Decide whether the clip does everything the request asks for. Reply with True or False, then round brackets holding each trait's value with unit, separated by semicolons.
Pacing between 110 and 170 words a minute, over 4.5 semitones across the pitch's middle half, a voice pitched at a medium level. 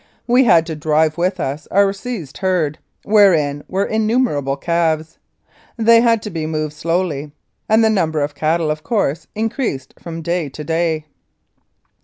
True (155 wpm; 4.9 semitones; 165 Hz)